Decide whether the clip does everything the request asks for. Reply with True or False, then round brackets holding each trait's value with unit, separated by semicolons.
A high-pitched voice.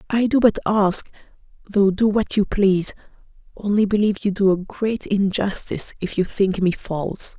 True (200 Hz)